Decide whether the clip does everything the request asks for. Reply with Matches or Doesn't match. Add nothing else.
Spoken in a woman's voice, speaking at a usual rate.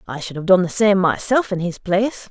Doesn't match